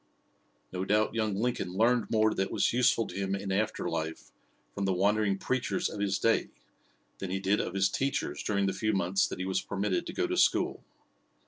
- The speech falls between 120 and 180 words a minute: No, fast, 205 wpm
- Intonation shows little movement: Yes, narrow, 2.3 semitones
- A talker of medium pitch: No, low, 100 Hz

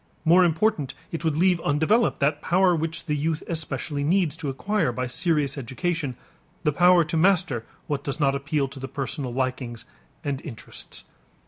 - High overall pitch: No, medium, 150 Hz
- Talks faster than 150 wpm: Yes, average, 165 wpm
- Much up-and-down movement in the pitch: No, average, 3.9 semitones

